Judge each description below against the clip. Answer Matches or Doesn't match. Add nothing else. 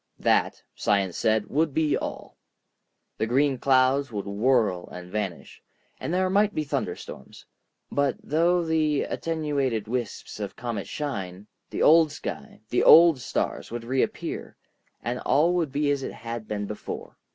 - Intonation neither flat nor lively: Doesn't match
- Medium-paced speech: Matches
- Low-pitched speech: Matches